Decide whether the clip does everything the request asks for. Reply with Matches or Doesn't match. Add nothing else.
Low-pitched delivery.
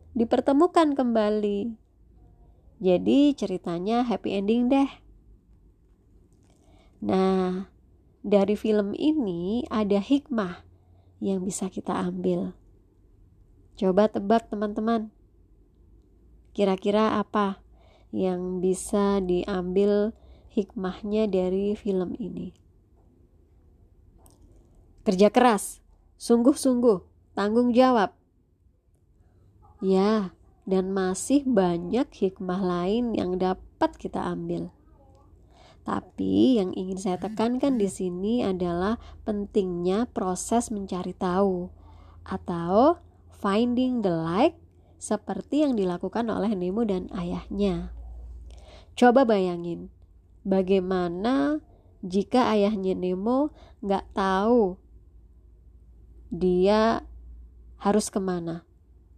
Doesn't match